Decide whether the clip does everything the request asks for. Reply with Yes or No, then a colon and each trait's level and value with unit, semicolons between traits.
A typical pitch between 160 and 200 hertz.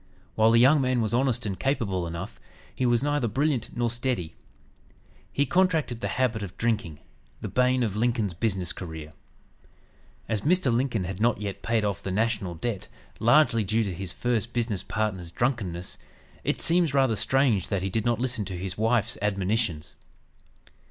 No: low, 115 Hz